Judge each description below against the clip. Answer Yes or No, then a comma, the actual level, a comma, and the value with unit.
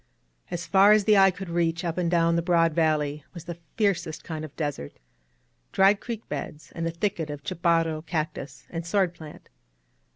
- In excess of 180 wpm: Yes, average, 195 wpm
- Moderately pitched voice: Yes, medium, 165 Hz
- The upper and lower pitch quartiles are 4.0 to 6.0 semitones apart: No, narrow, 2.5 semitones